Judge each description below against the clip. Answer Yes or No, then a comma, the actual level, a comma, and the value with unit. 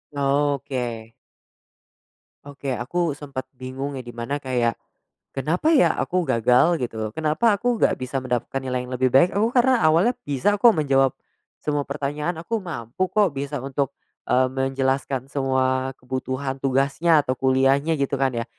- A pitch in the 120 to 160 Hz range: Yes, low, 135 Hz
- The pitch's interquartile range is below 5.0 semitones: Yes, average, 3.0 semitones